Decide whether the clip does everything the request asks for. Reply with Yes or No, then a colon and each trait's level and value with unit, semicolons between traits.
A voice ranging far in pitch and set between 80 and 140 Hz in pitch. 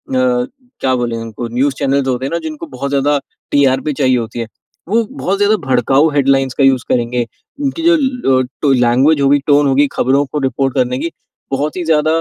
No: narrow, 2.6 semitones; low, 135 Hz